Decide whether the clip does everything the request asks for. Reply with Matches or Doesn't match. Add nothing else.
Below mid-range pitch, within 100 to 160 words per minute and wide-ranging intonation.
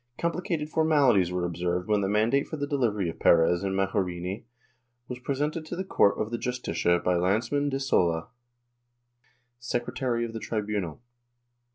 Matches